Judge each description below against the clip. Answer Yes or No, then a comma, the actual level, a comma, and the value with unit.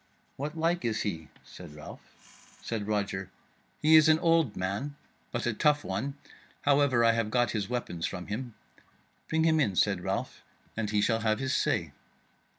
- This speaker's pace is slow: No, average, 170 wpm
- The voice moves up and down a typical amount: No, wide, 5.9 semitones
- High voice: No, low, 115 Hz